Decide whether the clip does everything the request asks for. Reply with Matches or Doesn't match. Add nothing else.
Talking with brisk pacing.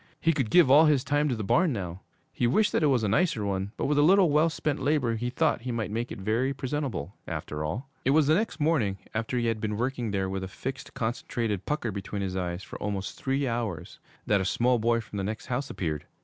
Matches